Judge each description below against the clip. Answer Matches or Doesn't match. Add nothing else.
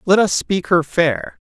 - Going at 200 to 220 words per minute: Matches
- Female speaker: Doesn't match